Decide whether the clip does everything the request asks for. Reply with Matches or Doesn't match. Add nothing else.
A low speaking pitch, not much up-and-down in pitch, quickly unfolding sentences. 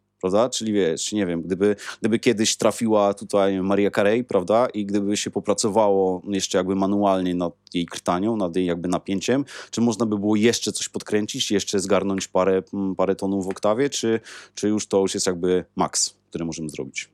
Matches